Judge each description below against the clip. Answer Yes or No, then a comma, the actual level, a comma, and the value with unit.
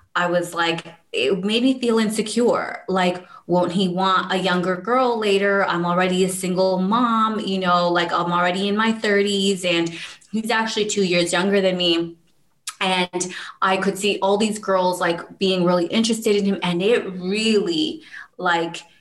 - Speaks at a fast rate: No, average, 170 wpm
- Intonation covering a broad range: No, average, 2.9 semitones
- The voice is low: No, high, 190 Hz